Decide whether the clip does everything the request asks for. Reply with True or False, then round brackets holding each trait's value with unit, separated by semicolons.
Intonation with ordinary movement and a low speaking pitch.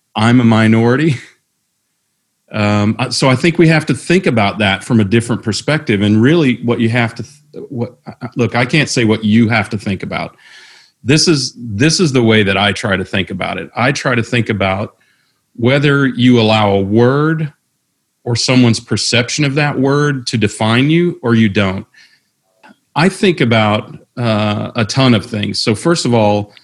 True (4.3 semitones; 120 Hz)